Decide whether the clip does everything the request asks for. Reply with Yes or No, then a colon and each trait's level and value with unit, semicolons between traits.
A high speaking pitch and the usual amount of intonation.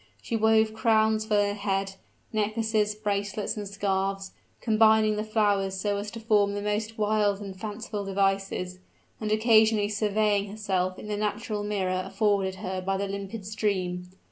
No: high, 205 Hz; narrow, 1.7 semitones